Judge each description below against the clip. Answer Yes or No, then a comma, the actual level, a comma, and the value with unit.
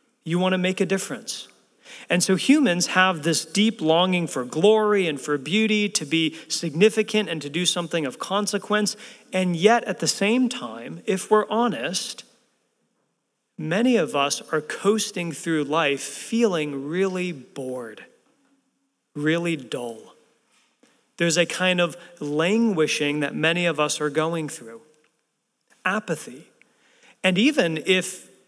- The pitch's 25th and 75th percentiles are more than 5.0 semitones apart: Yes, wide, 5.6 semitones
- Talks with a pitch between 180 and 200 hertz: Yes, medium, 185 Hz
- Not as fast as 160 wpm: Yes, slow, 135 wpm